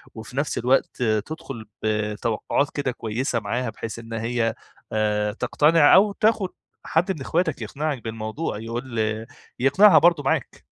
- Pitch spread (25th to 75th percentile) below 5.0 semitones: No, average, 5.3 semitones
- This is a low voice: Yes, low, 125 Hz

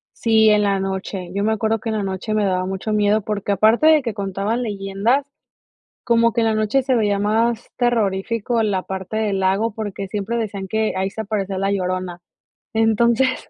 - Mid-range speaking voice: No, high, 210 Hz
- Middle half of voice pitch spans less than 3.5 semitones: Yes, narrow, 2.5 semitones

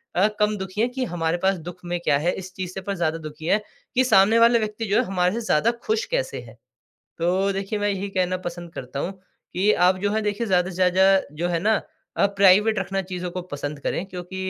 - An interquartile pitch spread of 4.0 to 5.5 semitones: No, average, 2.8 semitones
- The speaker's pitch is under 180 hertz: No, high, 190 Hz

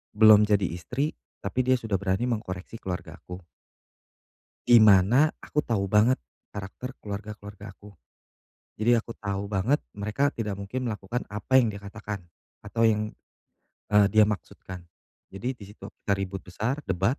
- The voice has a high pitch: No, low, 105 Hz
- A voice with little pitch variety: No, average, 3.0 semitones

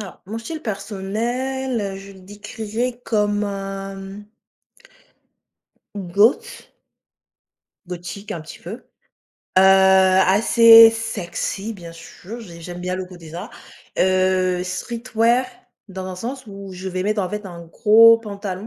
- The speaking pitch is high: Yes, high, 200 Hz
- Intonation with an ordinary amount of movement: Yes, average, 3.5 semitones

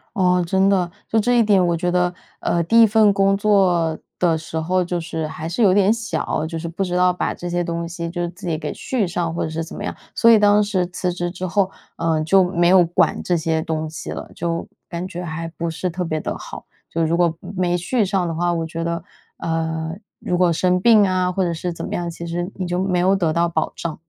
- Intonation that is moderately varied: No, narrow, 2.2 semitones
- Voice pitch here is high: No, medium, 175 Hz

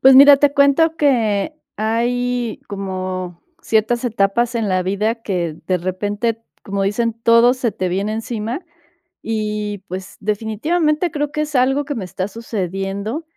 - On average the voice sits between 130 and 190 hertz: No, high, 220 Hz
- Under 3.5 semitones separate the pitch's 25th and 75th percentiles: No, average, 4.2 semitones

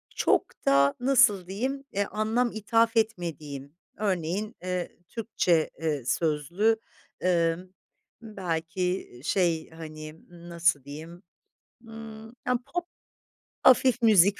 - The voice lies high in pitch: No, medium, 180 Hz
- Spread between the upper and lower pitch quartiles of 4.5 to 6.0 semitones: Yes, wide, 5.4 semitones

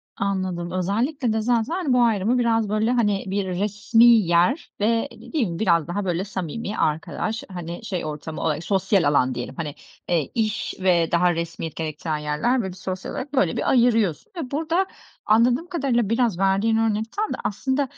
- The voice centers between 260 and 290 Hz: No, high, 205 Hz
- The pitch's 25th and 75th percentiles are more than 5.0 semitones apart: Yes, wide, 5.5 semitones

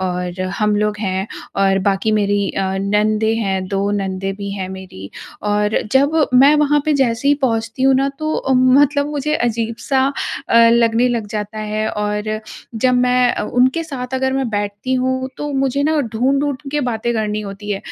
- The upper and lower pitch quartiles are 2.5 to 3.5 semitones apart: No, average, 4.2 semitones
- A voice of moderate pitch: No, high, 225 Hz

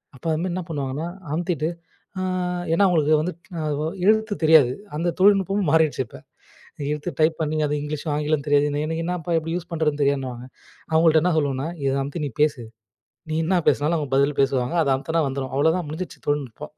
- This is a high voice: No, medium, 155 Hz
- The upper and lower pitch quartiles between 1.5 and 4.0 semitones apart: Yes, average, 2.8 semitones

